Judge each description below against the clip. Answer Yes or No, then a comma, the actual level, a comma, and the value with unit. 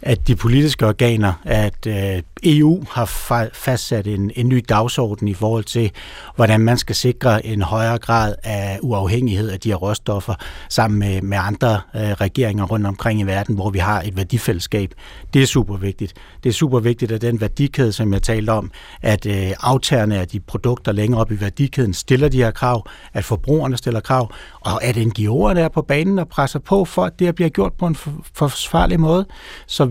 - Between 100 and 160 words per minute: No, average, 190 wpm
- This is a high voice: No, low, 115 Hz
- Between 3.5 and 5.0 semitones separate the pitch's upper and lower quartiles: Yes, average, 4.0 semitones